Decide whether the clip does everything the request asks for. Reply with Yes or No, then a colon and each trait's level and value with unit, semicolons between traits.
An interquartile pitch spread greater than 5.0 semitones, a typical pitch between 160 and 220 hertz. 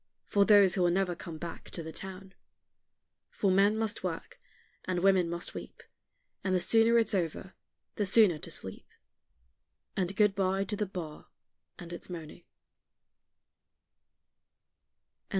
No: narrow, 2.6 semitones; high, 190 Hz